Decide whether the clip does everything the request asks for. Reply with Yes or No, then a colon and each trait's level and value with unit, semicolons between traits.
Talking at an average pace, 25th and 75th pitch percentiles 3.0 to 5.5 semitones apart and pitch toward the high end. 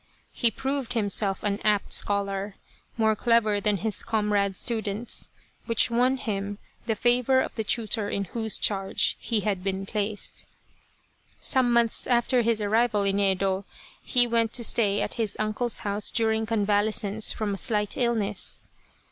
No: average, 150 wpm; narrow, 2.5 semitones; high, 215 Hz